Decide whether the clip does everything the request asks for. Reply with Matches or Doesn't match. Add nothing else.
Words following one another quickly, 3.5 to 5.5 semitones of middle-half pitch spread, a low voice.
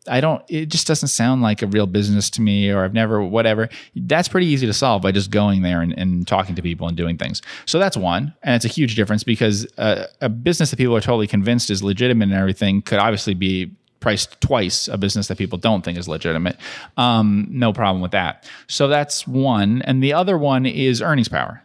Matches